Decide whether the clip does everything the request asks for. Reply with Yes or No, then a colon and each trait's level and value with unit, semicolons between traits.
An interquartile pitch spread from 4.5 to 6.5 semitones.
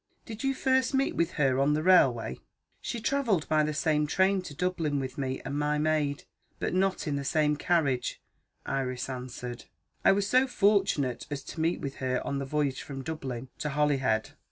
Yes: average, 5.2 semitones